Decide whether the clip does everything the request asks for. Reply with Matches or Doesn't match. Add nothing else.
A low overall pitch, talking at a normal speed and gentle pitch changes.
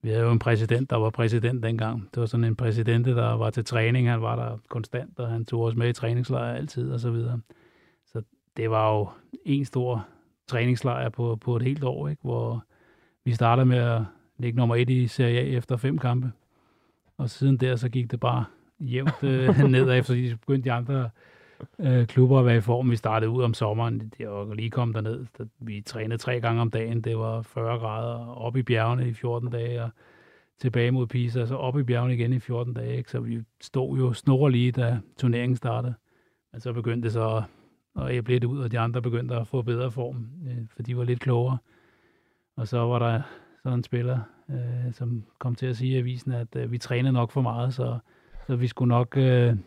Matches